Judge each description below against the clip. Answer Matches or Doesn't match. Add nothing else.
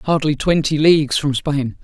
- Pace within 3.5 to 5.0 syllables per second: Matches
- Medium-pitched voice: Matches